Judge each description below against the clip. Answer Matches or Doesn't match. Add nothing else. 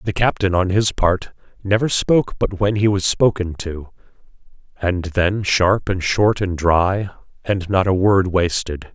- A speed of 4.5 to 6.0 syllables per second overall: Doesn't match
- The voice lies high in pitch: Doesn't match